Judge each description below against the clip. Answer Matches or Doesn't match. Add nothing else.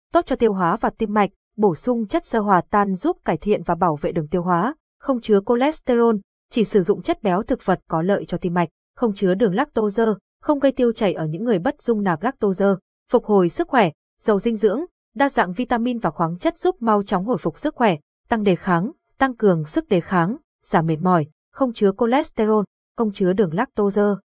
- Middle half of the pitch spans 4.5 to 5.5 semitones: Matches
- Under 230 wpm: Matches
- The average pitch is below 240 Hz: Matches